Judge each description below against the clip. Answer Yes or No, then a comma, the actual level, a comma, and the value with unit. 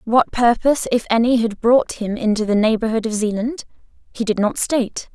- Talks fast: No, average, 185 wpm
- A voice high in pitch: Yes, high, 225 Hz